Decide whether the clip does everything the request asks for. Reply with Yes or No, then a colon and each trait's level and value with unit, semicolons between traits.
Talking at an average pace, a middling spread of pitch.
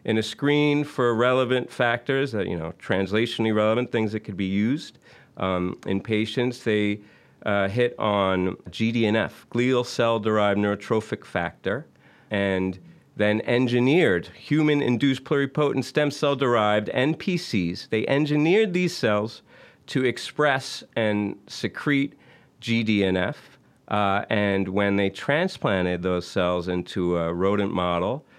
No: slow, 120 wpm; average, 4.8 semitones